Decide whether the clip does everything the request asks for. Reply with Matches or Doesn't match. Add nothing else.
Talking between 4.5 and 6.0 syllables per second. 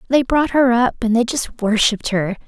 Matches